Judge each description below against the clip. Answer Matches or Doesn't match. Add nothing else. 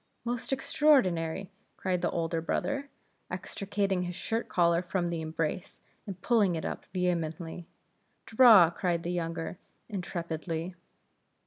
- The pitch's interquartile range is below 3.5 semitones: Matches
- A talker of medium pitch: Matches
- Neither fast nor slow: Doesn't match